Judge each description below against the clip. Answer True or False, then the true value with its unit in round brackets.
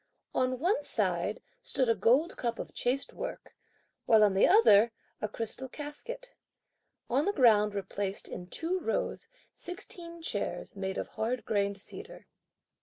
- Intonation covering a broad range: True (8.3 semitones)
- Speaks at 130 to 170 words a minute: True (150 wpm)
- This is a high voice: True (250 Hz)